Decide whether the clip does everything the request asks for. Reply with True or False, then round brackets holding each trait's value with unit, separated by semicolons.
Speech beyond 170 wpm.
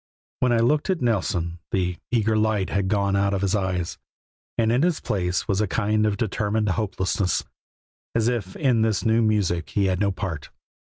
True (185 wpm)